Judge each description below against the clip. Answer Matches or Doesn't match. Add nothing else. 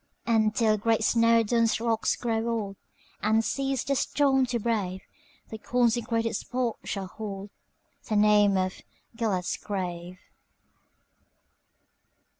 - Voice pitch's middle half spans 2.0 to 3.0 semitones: Matches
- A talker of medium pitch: Doesn't match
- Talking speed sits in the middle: Doesn't match